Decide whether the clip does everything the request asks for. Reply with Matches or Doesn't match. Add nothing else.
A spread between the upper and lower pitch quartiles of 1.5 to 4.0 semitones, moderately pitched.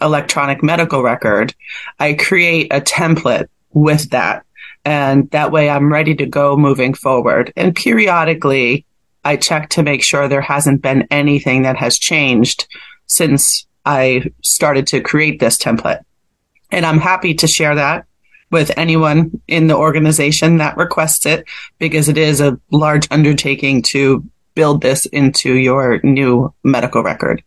Matches